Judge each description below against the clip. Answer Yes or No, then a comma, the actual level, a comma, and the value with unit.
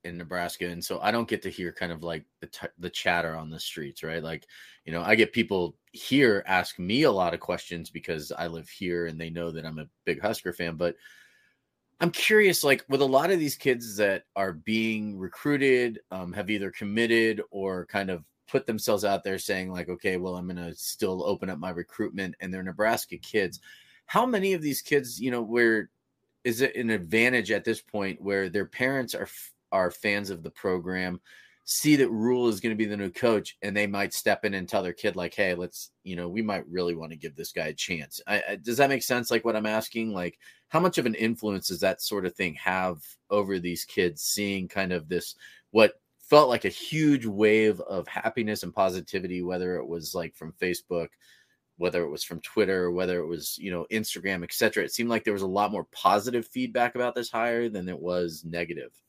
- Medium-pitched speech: No, low, 100 Hz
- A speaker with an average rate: No, fast, 225 wpm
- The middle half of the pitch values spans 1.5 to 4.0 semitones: No, average, 4.6 semitones